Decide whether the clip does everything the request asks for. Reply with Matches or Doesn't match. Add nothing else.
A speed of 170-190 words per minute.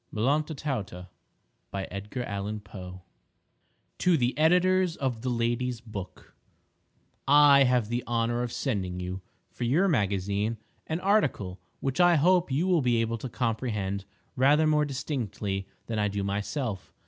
Doesn't match